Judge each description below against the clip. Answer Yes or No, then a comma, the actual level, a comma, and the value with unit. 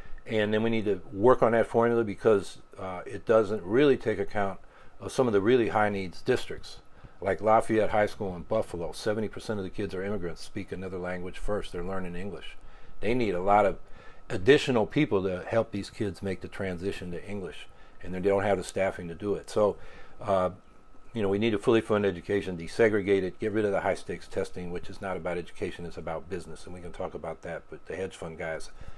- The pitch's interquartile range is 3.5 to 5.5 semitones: No, narrow, 2.6 semitones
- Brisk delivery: Yes, fast, 220 wpm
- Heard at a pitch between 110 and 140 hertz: No, low, 100 Hz